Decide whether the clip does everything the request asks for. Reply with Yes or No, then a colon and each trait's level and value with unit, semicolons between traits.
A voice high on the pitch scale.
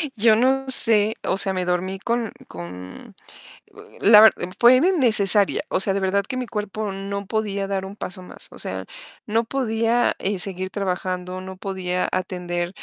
Yes: high, 200 Hz